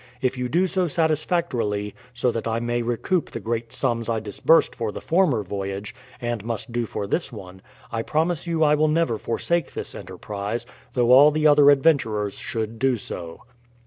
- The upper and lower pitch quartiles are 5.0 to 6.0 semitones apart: Yes, wide, 5.6 semitones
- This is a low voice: Yes, low, 120 Hz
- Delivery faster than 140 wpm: Yes, average, 180 wpm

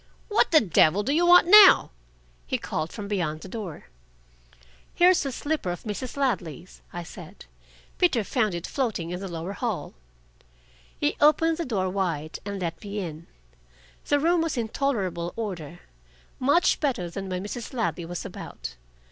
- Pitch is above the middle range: Yes, high, 205 Hz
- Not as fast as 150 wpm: No, average, 165 wpm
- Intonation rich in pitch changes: Yes, wide, 8.1 semitones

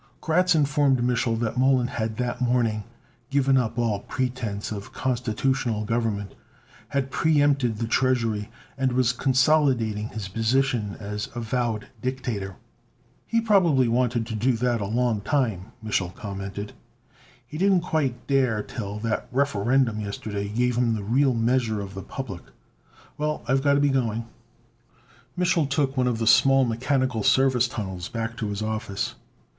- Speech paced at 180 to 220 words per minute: No, average, 150 wpm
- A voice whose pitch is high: No, low, 120 Hz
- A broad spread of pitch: No, average, 3.6 semitones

